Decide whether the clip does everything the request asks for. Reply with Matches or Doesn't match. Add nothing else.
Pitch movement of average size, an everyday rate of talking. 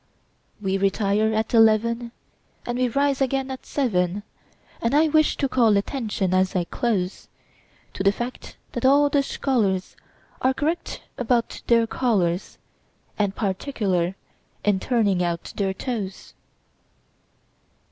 Doesn't match